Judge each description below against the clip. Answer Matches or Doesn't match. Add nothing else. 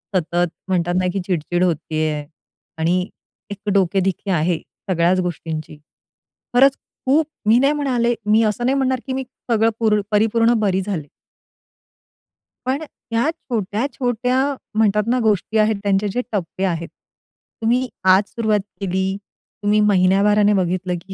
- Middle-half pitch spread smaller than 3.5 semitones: Doesn't match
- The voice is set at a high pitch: Matches